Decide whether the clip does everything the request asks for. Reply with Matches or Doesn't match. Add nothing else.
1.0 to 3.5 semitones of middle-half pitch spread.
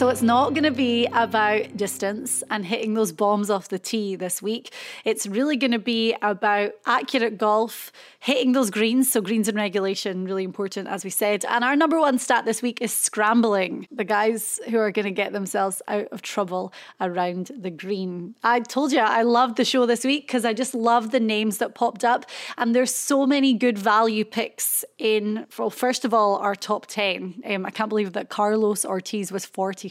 Matches